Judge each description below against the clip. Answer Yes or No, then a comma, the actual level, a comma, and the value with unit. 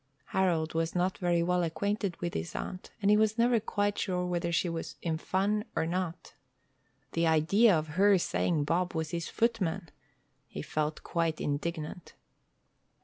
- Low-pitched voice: No, medium, 175 Hz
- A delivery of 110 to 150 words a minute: No, average, 160 wpm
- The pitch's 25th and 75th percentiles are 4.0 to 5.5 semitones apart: No, average, 3.2 semitones